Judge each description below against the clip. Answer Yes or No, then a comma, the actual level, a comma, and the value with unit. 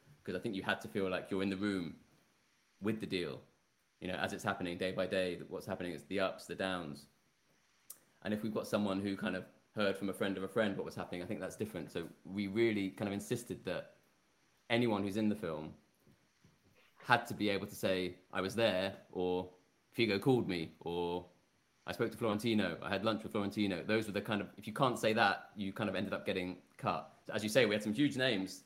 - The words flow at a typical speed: No, fast, 235 wpm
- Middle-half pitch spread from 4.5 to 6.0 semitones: No, average, 2.7 semitones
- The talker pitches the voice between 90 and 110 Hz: Yes, low, 100 Hz